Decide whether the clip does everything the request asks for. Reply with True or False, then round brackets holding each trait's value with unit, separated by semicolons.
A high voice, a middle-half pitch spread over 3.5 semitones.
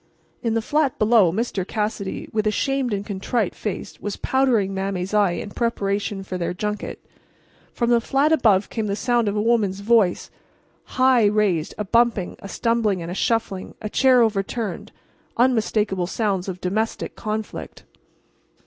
False (210 Hz; 3.2 semitones)